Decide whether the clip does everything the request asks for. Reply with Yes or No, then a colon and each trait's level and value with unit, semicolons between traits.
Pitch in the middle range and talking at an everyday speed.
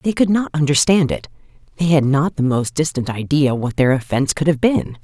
No: medium, 145 Hz; fast, 215 wpm